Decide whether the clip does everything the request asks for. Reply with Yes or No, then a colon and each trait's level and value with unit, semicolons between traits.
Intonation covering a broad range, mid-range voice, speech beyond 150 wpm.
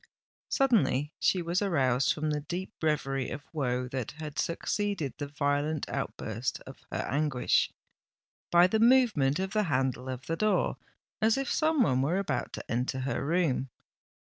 Yes: wide, 6.0 semitones; medium, 150 Hz; average, 160 wpm